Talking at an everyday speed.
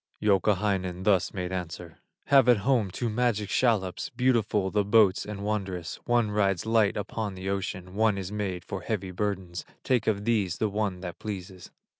Yes: average, 170 wpm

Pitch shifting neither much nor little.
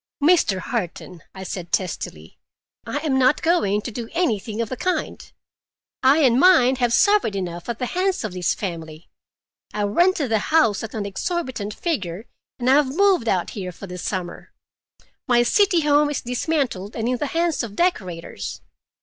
No: wide, 7.5 semitones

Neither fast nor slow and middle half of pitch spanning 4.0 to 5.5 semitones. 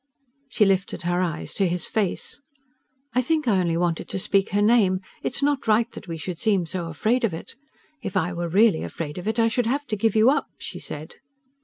No: fast, 220 wpm; average, 4.7 semitones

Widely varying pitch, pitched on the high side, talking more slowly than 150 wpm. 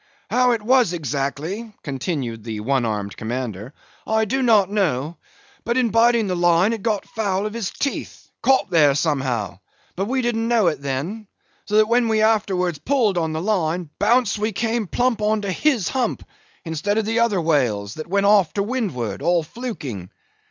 No: wide, 7.4 semitones; high, 195 Hz; average, 180 wpm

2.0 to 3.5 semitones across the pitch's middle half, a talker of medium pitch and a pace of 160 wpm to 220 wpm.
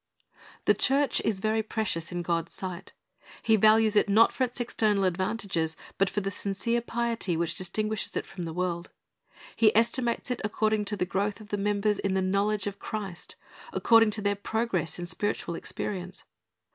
No: average, 3.0 semitones; high, 205 Hz; average, 180 wpm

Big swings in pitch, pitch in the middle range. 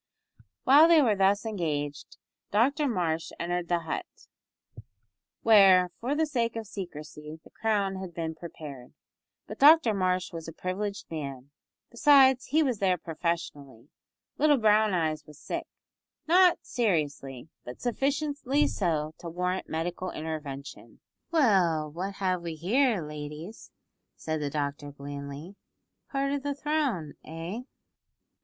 Yes: wide, 7.1 semitones; medium, 180 Hz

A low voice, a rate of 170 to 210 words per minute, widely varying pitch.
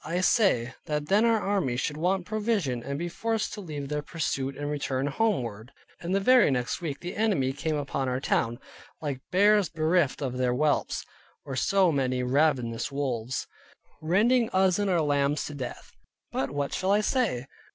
No: medium, 150 Hz; average, 180 wpm; wide, 6.3 semitones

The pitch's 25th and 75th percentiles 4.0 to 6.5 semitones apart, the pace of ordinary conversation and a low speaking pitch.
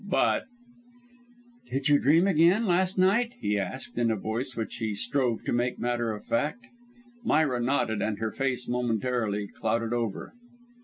Yes: average, 4.6 semitones; average, 155 wpm; low, 120 Hz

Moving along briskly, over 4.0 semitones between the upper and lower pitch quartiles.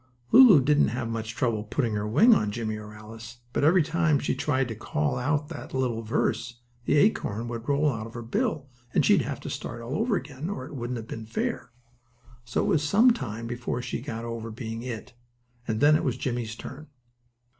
Yes: fast, 210 wpm; average, 4.4 semitones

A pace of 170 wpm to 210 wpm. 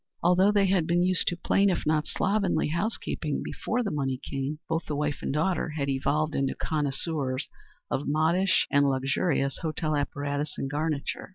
Yes: average, 175 wpm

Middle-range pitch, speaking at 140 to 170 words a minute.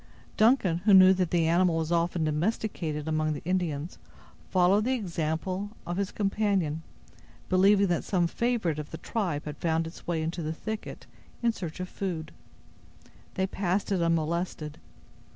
Yes: medium, 175 Hz; average, 155 wpm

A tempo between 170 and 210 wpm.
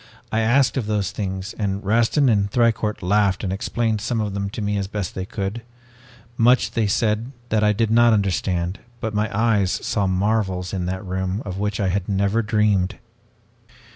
Yes: average, 185 wpm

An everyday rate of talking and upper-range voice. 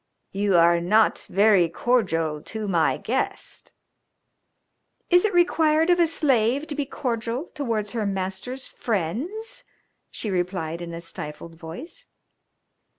No: slow, 125 wpm; high, 215 Hz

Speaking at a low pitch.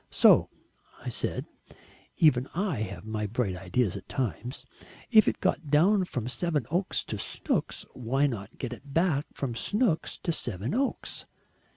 Yes: low, 130 Hz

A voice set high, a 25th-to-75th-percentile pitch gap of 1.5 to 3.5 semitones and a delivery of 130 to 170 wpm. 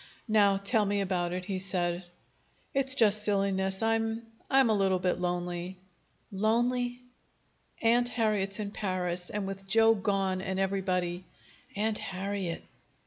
Yes: high, 195 Hz; average, 3.0 semitones; average, 140 wpm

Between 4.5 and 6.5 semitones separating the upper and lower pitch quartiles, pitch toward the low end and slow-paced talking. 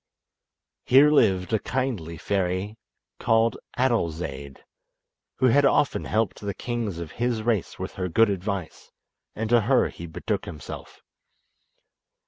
Yes: average, 5.1 semitones; low, 105 Hz; slow, 125 wpm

